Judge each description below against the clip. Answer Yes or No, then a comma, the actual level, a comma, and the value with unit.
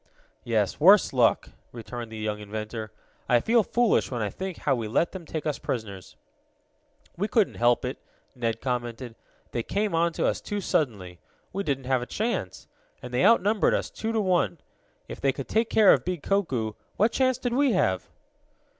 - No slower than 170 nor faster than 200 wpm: Yes, average, 180 wpm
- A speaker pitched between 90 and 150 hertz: Yes, low, 135 Hz